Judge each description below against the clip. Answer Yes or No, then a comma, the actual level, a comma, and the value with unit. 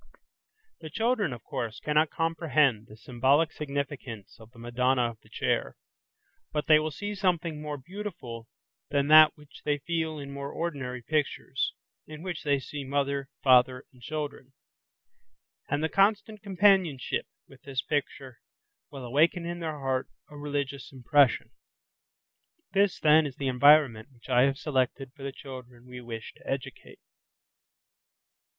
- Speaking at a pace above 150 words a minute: No, average, 145 wpm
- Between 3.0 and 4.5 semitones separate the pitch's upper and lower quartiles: Yes, average, 3.5 semitones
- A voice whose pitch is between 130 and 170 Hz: Yes, medium, 140 Hz